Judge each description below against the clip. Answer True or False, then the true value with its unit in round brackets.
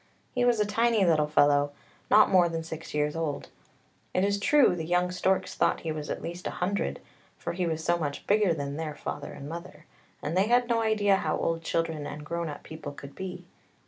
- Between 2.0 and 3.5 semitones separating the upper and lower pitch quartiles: False (4.4 semitones)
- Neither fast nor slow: False (215 wpm)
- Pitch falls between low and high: True (170 Hz)